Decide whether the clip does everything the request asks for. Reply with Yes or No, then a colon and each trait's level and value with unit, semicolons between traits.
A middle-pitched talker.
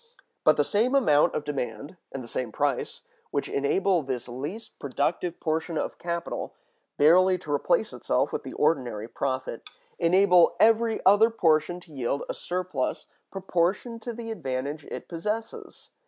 Yes: medium, 165 Hz